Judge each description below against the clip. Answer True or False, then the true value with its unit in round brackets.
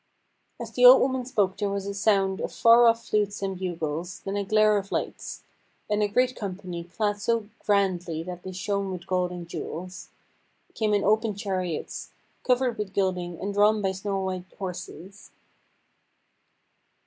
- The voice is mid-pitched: False (200 Hz)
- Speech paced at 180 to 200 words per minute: False (165 wpm)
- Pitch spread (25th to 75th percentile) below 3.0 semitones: True (2.5 semitones)